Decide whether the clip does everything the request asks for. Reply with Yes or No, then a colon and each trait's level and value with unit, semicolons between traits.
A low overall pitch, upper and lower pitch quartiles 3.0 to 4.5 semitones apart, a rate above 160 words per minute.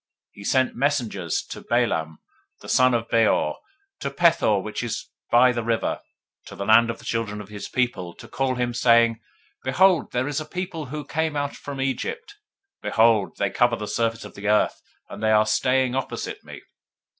Yes: low, 120 Hz; average, 3.7 semitones; average, 185 wpm